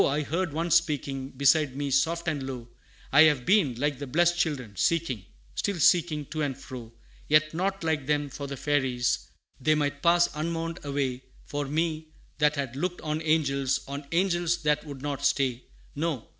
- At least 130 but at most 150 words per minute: No, average, 175 wpm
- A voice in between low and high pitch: Yes, medium, 145 Hz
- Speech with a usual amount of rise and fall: Yes, average, 3.2 semitones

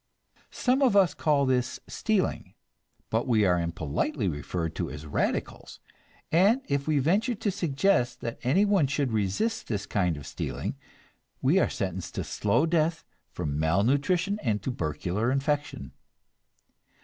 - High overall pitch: No, low, 130 Hz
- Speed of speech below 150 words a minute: Yes, slow, 135 wpm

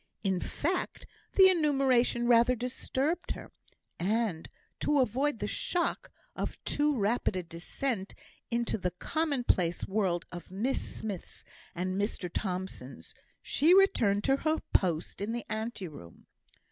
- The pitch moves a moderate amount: No, wide, 6.7 semitones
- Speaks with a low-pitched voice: No, high, 225 Hz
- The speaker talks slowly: Yes, slow, 130 wpm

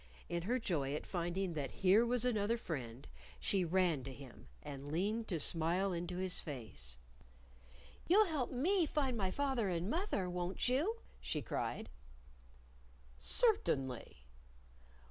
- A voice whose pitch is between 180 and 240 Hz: Yes, medium, 185 Hz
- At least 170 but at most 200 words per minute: No, average, 150 wpm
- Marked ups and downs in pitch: Yes, wide, 7.9 semitones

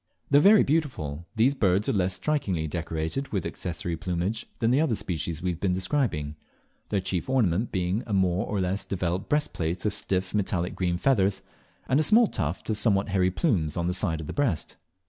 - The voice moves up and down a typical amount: Yes, average, 4.7 semitones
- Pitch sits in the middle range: No, very low, 95 Hz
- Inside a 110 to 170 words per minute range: No, average, 195 wpm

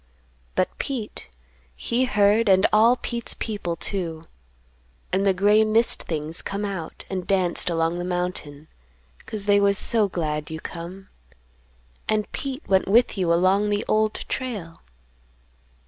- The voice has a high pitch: Yes, high, 195 Hz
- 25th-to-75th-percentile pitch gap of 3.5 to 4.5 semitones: Yes, average, 3.8 semitones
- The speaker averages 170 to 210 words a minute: No, average, 140 wpm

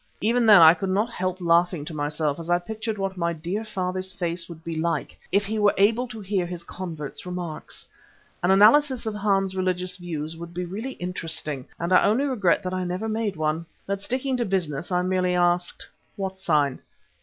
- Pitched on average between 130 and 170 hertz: No, medium, 185 Hz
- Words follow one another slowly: No, average, 200 wpm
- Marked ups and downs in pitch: No, average, 3.2 semitones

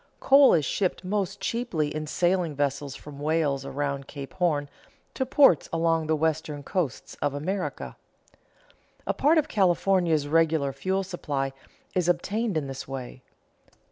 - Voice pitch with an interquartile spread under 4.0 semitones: No, average, 4.7 semitones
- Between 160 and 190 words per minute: No, average, 140 wpm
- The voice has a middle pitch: Yes, medium, 160 Hz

